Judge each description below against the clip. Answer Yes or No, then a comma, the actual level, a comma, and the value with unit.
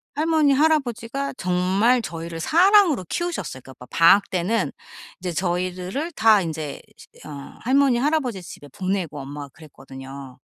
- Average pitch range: No, wide, 9.0 semitones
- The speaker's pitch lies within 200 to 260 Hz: No, high, 190 Hz